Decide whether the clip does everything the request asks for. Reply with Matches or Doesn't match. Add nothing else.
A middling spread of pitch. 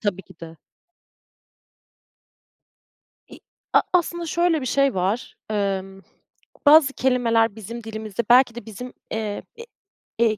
Matches